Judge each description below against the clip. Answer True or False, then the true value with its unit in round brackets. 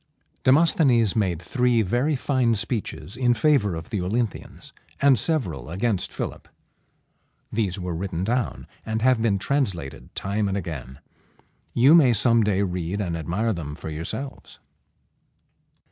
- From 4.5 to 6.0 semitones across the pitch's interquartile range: True (5.6 semitones)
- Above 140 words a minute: False (135 wpm)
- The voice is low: True (105 Hz)